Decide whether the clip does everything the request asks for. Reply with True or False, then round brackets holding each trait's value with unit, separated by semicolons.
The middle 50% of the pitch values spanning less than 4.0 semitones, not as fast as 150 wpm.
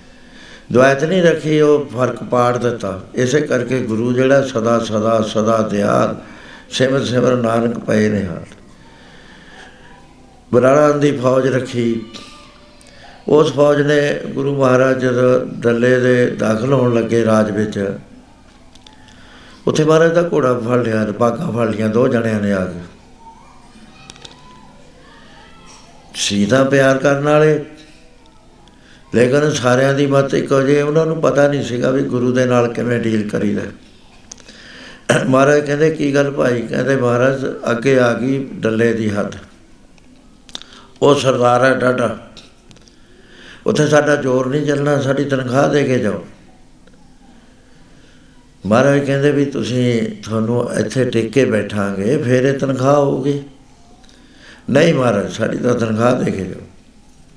True (3.3 semitones; 125 wpm)